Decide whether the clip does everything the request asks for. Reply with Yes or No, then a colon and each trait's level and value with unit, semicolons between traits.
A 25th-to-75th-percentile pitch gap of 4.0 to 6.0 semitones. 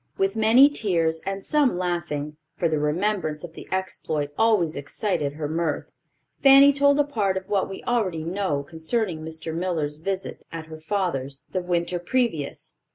Yes: average, 4.5 semitones